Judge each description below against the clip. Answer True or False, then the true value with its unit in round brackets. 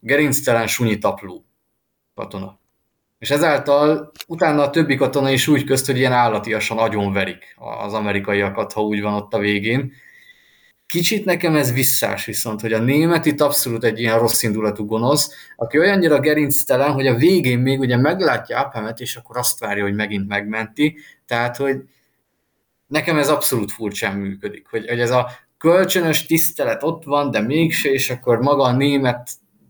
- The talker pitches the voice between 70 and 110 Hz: False (130 Hz)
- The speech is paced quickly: True (160 wpm)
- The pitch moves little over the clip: False (5.0 semitones)